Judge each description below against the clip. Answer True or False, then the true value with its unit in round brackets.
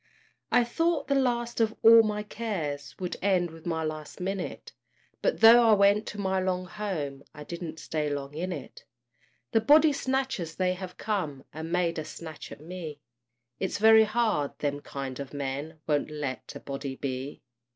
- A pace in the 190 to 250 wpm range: False (175 wpm)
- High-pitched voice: False (180 Hz)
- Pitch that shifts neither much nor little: False (6.6 semitones)